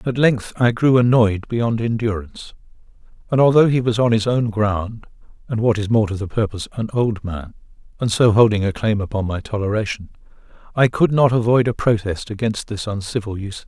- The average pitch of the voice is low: Yes, low, 110 Hz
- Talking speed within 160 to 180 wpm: No, average, 190 wpm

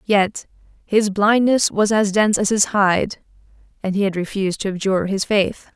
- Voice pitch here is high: Yes, high, 200 Hz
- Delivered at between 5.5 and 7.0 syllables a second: No, 4.9 syllables/s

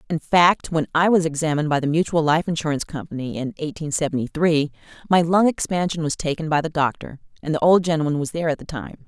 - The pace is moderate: No, fast, 220 wpm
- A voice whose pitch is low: No, medium, 160 Hz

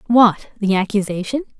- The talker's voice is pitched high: Yes, high, 215 Hz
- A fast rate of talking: No, slow, 115 wpm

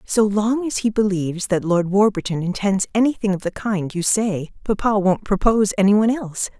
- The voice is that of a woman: Yes, female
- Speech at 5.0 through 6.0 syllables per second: Yes, 5.5 syllables/s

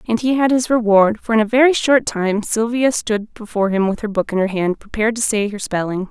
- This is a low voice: No, high, 220 Hz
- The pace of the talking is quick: Yes, fast, 255 wpm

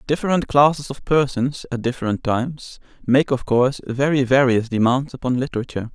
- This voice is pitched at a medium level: No, low, 130 Hz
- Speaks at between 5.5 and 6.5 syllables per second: Yes, 5.6 syllables/s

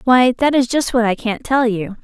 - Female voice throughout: Yes, female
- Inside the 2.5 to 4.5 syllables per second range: No, 4.9 syllables/s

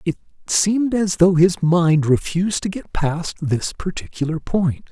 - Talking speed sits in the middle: Yes, average, 160 wpm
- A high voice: No, medium, 175 Hz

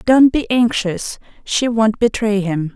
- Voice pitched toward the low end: No, high, 220 Hz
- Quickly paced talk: No, average, 155 wpm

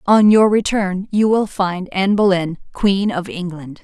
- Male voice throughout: No, female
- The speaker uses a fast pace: No, average, 170 wpm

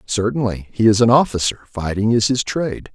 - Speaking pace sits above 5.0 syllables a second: Yes, 5.5 syllables/s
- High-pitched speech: No, low, 115 Hz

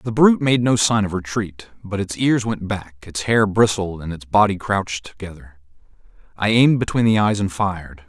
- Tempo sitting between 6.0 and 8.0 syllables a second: No, 5.2 syllables/s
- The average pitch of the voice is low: Yes, low, 100 Hz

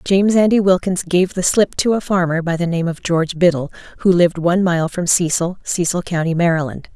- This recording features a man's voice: No, female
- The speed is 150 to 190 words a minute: No, fast, 205 wpm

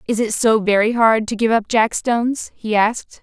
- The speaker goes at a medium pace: No, fast, 225 wpm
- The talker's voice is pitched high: Yes, high, 220 Hz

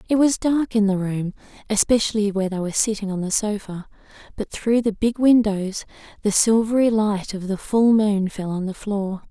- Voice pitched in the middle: No, high, 210 Hz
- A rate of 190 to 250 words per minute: Yes, average, 195 wpm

